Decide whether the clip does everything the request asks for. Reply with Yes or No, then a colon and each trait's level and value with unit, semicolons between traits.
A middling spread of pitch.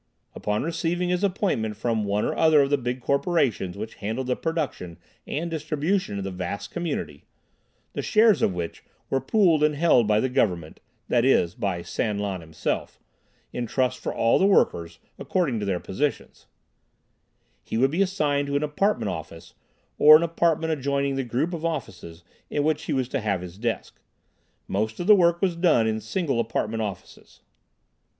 No: wide, 7.6 semitones